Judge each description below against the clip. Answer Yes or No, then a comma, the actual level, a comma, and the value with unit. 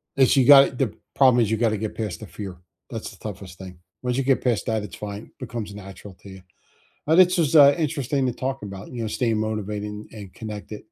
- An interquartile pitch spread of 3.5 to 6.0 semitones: Yes, average, 4.2 semitones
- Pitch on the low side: Yes, low, 110 Hz